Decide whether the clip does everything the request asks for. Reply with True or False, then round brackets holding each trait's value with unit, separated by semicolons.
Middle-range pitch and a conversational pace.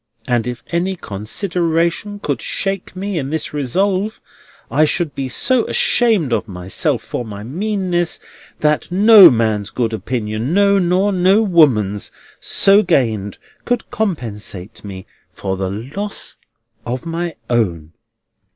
False (155 Hz; 125 wpm)